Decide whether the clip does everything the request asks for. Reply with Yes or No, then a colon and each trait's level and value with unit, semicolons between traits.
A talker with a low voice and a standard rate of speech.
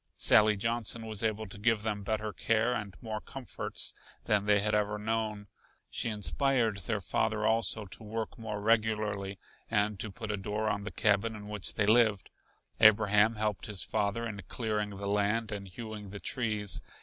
Yes: low, 105 Hz; average, 175 wpm